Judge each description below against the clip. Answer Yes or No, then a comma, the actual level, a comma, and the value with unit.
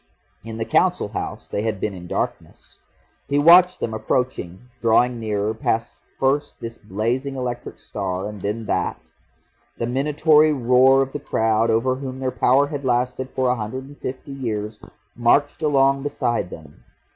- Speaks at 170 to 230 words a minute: No, average, 160 wpm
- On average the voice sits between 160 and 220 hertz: No, low, 125 Hz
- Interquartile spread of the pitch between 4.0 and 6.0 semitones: No, average, 3.5 semitones